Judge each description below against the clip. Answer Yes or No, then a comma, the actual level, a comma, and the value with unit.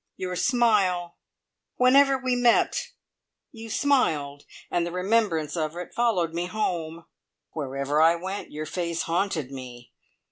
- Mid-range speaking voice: Yes, medium, 175 Hz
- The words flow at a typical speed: No, slow, 130 wpm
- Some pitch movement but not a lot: No, wide, 6.0 semitones